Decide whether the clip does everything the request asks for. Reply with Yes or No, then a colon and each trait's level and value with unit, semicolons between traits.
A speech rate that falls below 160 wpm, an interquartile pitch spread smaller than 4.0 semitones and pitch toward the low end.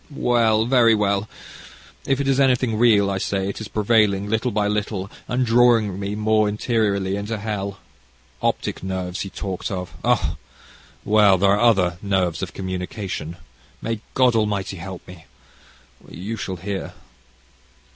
Yes: average, 145 wpm; average, 2.8 semitones; low, 105 Hz